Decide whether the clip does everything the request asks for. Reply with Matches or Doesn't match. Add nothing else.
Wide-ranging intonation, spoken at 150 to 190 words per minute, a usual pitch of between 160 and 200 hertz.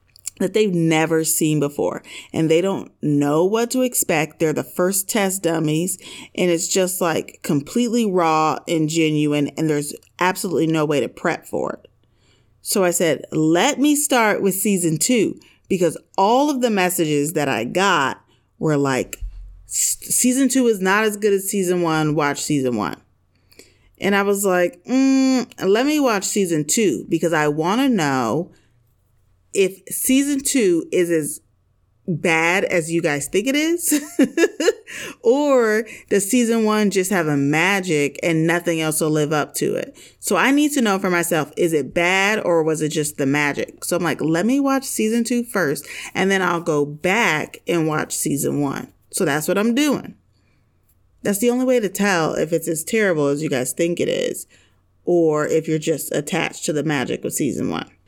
Matches